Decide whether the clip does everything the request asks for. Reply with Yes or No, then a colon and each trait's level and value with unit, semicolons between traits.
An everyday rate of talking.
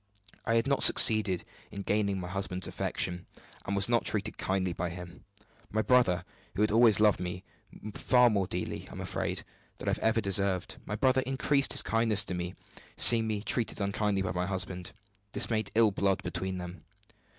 Yes: average, 185 wpm